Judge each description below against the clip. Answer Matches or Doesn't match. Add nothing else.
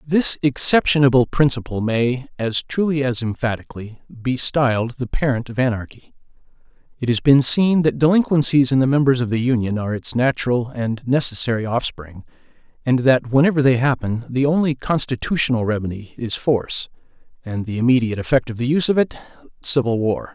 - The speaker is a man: Matches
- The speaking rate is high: Doesn't match